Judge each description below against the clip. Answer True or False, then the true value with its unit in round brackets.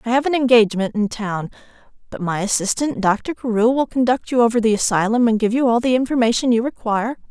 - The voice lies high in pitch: True (230 Hz)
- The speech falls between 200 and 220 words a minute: True (205 wpm)